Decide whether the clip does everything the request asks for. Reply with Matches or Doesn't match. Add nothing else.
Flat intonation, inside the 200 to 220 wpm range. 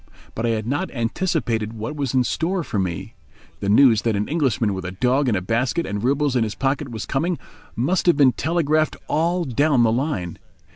Doesn't match